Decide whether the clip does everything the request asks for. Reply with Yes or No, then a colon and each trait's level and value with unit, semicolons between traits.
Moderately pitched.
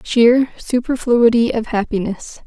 No: high, 235 Hz